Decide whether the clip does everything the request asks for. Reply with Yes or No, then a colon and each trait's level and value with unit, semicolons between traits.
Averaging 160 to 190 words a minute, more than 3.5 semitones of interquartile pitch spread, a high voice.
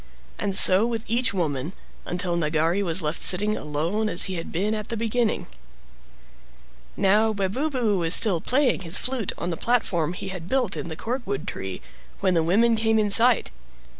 Yes: average, 175 wpm; average, 4.8 semitones; high, 195 Hz